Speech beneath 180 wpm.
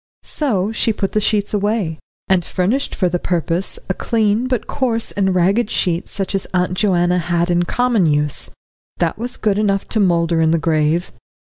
No: average, 185 wpm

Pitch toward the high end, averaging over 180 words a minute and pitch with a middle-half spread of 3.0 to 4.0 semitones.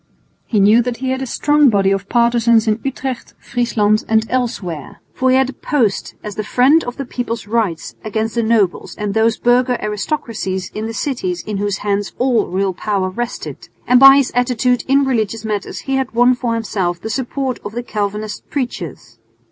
Yes: high, 230 Hz; average, 190 wpm; average, 3.5 semitones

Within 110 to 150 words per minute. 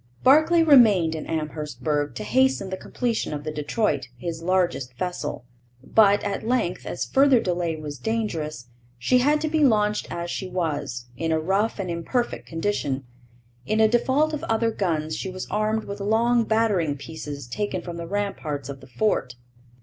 No: average, 165 wpm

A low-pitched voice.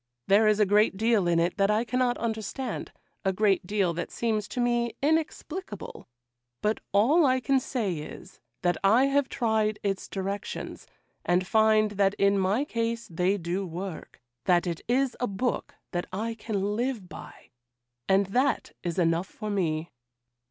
No: high, 210 Hz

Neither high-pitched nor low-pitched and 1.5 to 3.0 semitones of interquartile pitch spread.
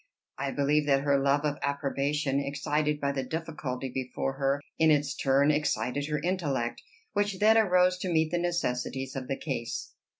Yes: medium, 145 Hz; average, 2.7 semitones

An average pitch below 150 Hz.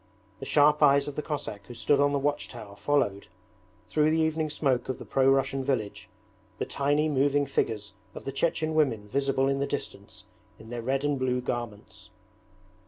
Yes: low, 135 Hz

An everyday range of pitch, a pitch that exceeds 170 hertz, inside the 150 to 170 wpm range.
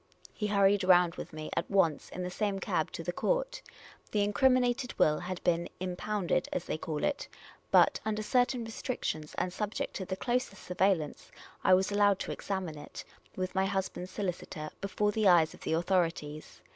No: average, 3.2 semitones; high, 190 Hz; average, 185 wpm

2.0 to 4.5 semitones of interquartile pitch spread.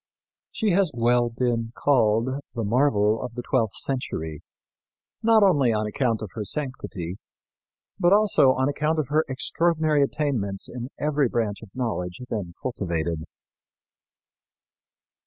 No: average, 5.3 semitones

